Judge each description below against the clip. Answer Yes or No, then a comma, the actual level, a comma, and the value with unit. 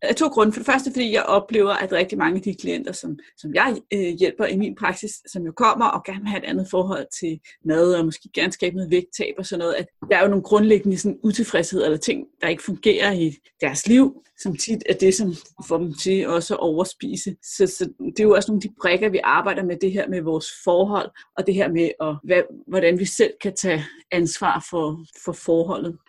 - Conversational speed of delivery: No, fast, 240 wpm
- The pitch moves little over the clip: No, average, 3.2 semitones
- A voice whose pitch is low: No, high, 190 Hz